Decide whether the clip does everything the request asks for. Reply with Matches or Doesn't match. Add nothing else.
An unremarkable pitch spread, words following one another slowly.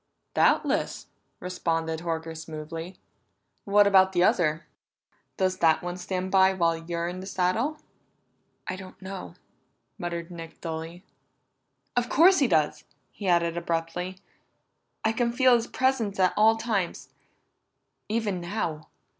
Matches